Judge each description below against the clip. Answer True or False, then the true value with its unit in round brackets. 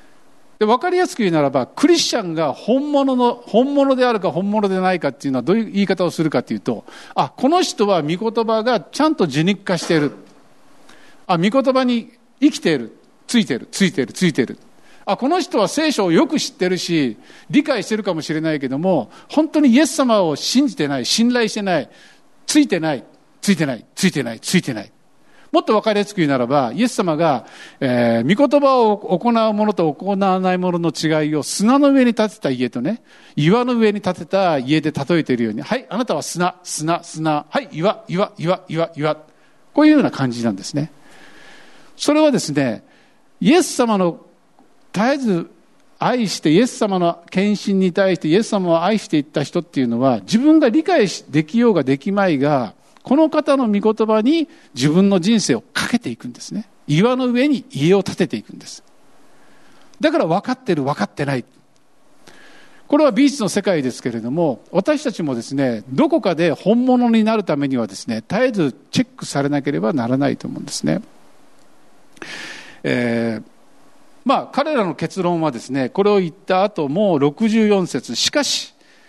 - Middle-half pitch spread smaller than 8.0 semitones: False (8.4 semitones)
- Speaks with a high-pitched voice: True (200 Hz)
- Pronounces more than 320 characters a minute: True (360 characters per minute)